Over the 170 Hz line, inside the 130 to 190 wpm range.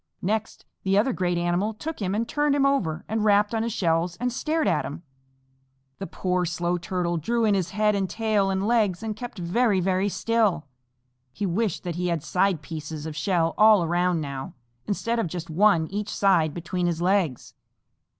No: high, 190 Hz; average, 200 wpm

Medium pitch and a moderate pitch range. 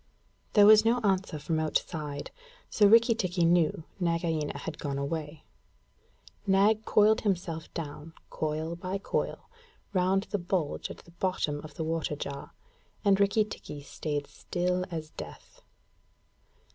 Yes: medium, 170 Hz; average, 4.1 semitones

